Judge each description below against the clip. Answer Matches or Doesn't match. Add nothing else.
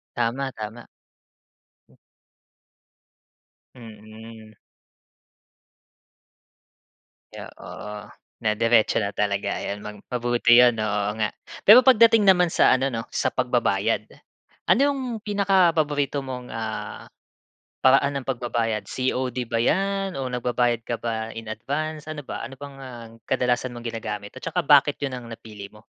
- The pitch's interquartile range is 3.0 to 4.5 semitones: Matches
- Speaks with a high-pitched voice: Doesn't match